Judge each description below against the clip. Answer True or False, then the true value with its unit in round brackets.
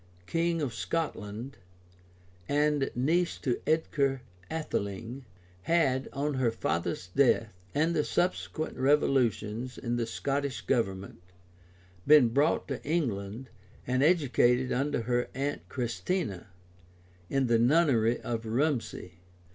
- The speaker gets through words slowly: True (110 wpm)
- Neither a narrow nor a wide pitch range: True (4.3 semitones)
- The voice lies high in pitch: False (130 Hz)